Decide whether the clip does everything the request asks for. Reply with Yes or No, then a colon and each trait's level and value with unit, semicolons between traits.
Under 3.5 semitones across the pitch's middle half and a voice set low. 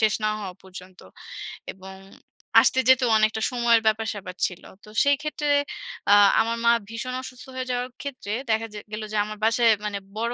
No: average, 2.8 semitones; high, 225 Hz